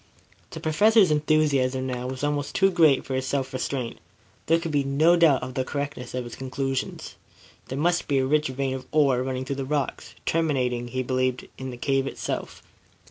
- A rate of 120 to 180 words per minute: No, average, 190 wpm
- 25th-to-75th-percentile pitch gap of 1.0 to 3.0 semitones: Yes, average, 2.7 semitones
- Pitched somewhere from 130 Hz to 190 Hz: Yes, low, 135 Hz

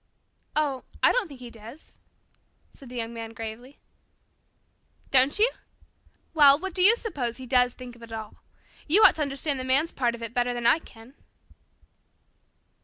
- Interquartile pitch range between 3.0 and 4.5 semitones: Yes, average, 4.0 semitones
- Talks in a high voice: Yes, very high, 255 Hz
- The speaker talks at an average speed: Yes, average, 175 wpm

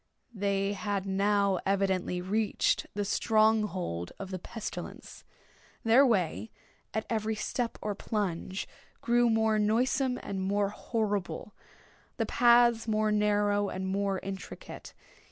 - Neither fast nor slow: No, slow, 120 wpm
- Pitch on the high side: Yes, high, 205 Hz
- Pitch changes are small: Yes, narrow, 2.2 semitones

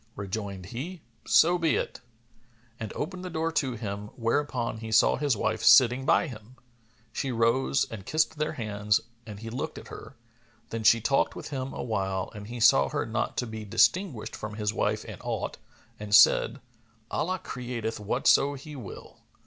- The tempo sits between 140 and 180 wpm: Yes, average, 175 wpm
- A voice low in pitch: Yes, low, 115 Hz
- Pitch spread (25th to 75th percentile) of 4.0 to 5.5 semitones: Yes, average, 4.8 semitones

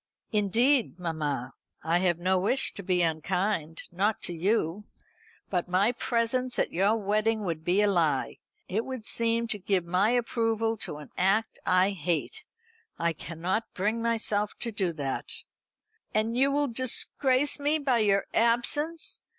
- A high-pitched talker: Yes, high, 205 Hz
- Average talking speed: Yes, average, 150 wpm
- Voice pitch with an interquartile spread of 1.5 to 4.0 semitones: No, average, 4.6 semitones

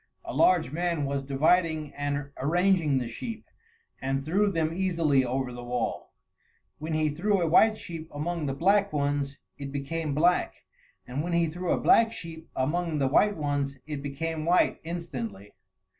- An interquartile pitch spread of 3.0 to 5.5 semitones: Yes, average, 3.8 semitones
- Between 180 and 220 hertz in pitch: No, medium, 155 Hz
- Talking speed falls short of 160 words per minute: No, average, 165 wpm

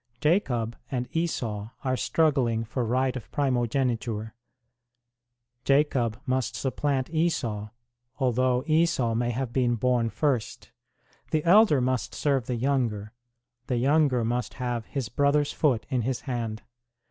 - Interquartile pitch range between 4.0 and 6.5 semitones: No, average, 3.3 semitones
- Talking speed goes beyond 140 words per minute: No, slow, 135 wpm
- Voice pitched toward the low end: Yes, low, 125 Hz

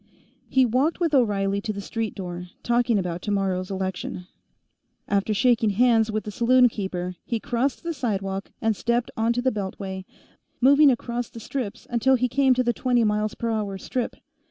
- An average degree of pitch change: Yes, average, 3.9 semitones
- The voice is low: No, high, 225 Hz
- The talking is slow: No, average, 165 wpm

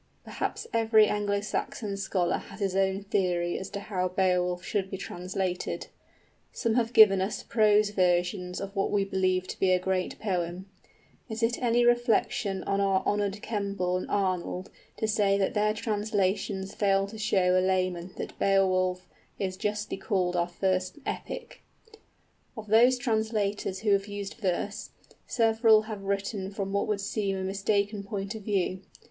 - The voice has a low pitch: No, high, 195 Hz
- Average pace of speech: Yes, average, 160 wpm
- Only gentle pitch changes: Yes, narrow, 2.2 semitones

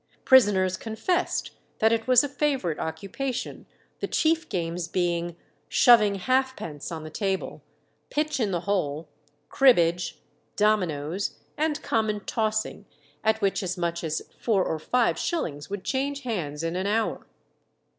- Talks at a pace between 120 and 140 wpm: Yes, slow, 135 wpm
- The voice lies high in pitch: Yes, high, 205 Hz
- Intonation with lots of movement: Yes, wide, 6.3 semitones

